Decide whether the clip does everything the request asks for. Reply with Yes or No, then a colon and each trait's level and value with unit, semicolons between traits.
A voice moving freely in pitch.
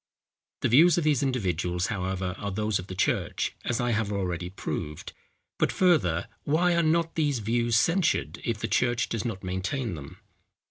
Yes: wide, 7.2 semitones